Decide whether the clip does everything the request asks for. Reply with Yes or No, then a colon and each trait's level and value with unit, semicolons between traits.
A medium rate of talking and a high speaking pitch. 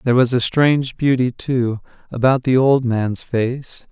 No: average, 170 wpm; low, 125 Hz